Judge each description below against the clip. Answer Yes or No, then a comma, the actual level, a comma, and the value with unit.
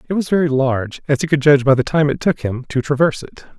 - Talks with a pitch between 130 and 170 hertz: Yes, medium, 140 Hz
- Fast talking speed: Yes, fast, 285 wpm